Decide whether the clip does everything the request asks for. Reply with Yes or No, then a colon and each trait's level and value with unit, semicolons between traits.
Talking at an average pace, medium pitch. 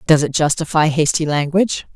Yes: average, 155 wpm; medium, 155 Hz